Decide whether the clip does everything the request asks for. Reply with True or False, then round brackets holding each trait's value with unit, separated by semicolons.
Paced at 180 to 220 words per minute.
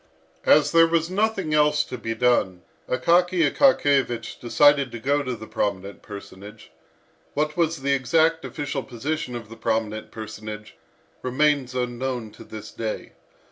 False (140 wpm)